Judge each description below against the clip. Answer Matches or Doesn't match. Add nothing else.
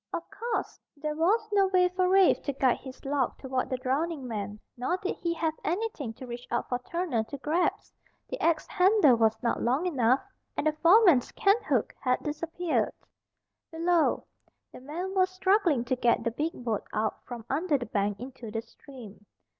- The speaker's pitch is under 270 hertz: Doesn't match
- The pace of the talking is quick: Doesn't match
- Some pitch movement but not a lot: Doesn't match